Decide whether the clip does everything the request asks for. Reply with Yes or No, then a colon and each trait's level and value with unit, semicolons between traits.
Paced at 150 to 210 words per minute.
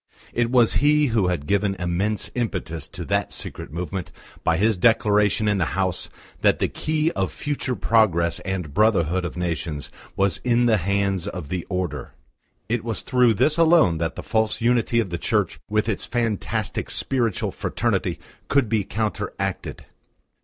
Yes: average, 160 wpm